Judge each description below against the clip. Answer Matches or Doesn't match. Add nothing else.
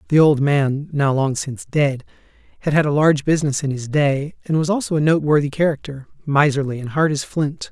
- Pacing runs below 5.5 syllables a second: Doesn't match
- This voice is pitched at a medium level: Matches